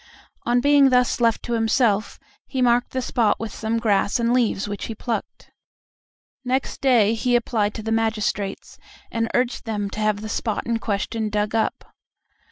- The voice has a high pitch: Yes, high, 225 Hz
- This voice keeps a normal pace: Yes, average, 175 wpm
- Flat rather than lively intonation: Yes, narrow, 2.3 semitones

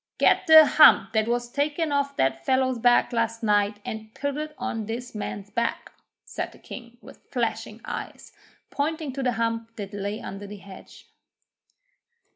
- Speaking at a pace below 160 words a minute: No, average, 165 wpm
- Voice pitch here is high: Yes, high, 235 Hz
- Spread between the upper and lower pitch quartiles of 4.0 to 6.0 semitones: Yes, average, 4.8 semitones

